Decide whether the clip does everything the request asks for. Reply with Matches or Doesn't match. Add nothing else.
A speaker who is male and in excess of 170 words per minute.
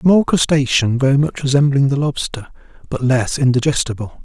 Doesn't match